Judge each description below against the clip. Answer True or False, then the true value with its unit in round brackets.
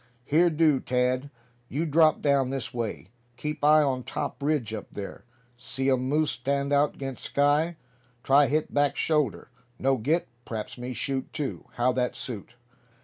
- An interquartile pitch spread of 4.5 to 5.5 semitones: False (3.0 semitones)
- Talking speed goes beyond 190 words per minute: False (160 wpm)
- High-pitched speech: False (135 Hz)